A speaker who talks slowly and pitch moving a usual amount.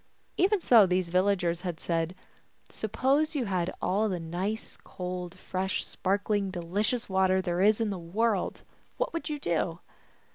No: average, 155 wpm; average, 3.5 semitones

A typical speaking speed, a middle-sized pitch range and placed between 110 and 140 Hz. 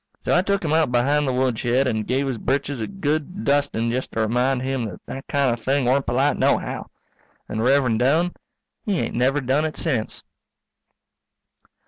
Yes: average, 180 wpm; average, 3.0 semitones; low, 135 Hz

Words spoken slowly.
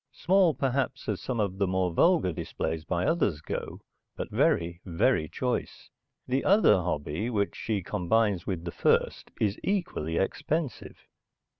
No: average, 145 wpm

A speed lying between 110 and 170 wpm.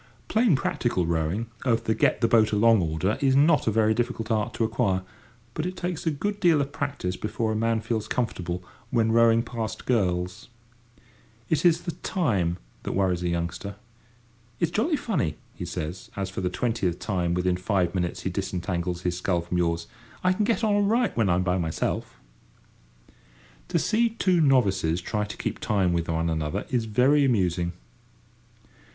No: average, 180 wpm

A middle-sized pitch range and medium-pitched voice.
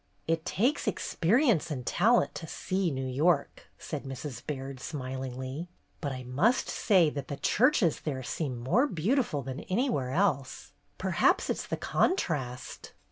No: wide, 6.3 semitones; medium, 150 Hz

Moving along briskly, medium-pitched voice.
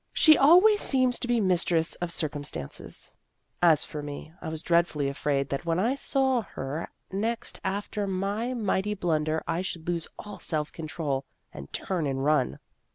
No: average, 160 wpm; medium, 170 Hz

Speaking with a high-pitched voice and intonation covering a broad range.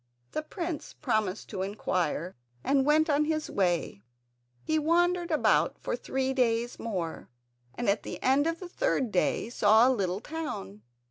Yes: very high, 250 Hz; wide, 7.8 semitones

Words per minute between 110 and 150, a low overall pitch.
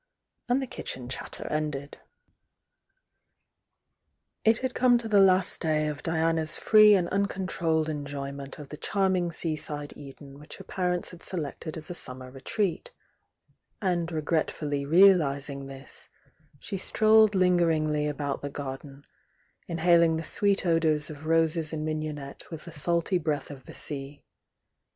No: average, 140 wpm; medium, 160 Hz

